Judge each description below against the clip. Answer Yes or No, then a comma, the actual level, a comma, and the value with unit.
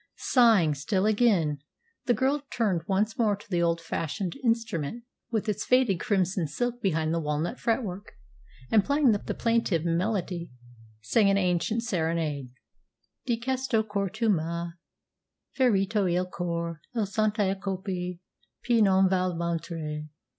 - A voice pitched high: Yes, high, 195 Hz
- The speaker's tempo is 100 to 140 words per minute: Yes, slow, 135 wpm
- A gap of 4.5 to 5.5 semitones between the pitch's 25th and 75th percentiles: Yes, average, 4.9 semitones